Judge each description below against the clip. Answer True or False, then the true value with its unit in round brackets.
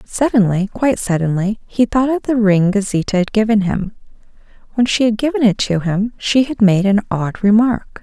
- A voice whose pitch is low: False (215 Hz)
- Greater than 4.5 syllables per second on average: True (5.1 syllables/s)